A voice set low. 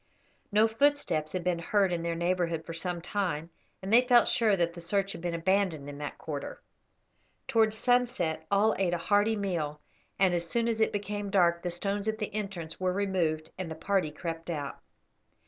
No: medium, 185 Hz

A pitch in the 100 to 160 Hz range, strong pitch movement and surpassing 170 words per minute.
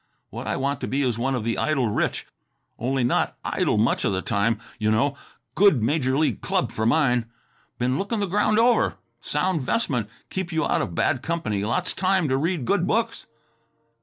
Yes: low, 135 Hz; wide, 7.0 semitones; average, 190 wpm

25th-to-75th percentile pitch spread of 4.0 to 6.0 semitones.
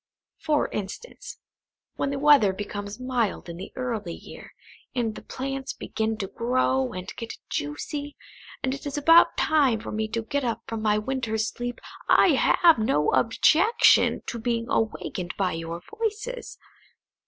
Yes: average, 4.7 semitones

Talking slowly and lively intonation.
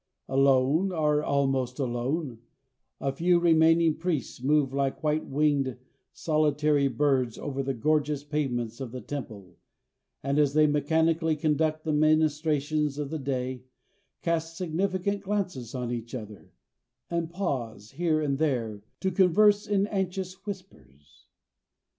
No: slow, 130 wpm; average, 3.5 semitones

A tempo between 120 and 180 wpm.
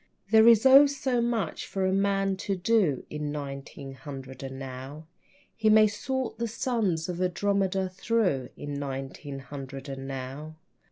Yes: average, 155 wpm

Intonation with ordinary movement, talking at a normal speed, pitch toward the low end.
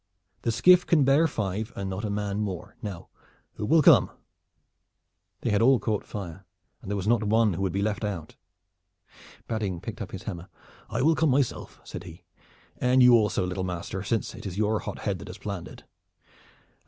Yes: average, 3.4 semitones; average, 195 wpm; low, 105 Hz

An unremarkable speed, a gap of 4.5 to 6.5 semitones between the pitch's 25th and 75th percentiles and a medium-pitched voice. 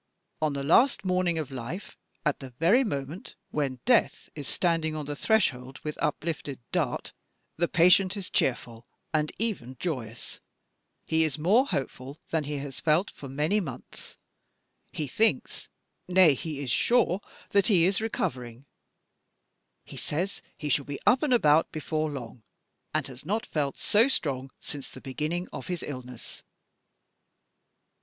Yes: average, 150 wpm; average, 5.1 semitones; medium, 155 Hz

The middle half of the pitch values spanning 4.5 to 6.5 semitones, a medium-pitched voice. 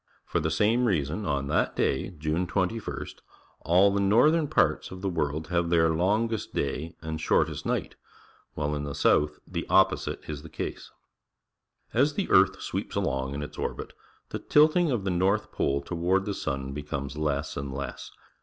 No: average, 5.3 semitones; very low, 85 Hz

